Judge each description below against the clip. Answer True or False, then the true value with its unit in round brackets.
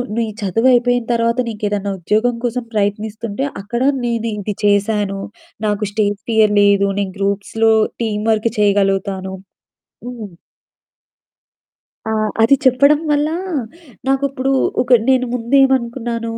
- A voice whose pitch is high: True (220 Hz)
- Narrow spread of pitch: False (3.2 semitones)